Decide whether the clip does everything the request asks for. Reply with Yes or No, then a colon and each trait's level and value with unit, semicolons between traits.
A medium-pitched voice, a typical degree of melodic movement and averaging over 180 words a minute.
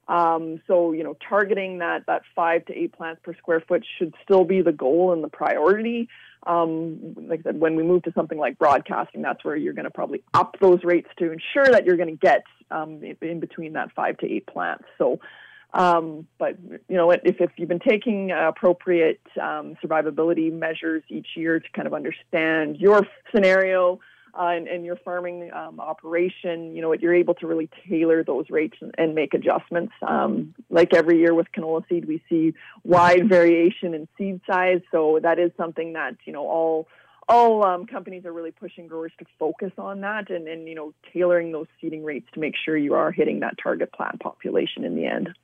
No: medium, 170 Hz; narrow, 1.9 semitones; fast, 205 wpm